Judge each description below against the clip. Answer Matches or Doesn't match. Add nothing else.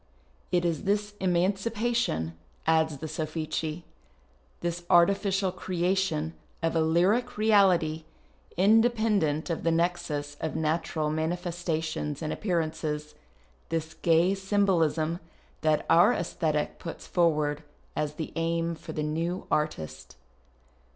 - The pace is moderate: Doesn't match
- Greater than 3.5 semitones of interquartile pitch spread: Doesn't match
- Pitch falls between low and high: Matches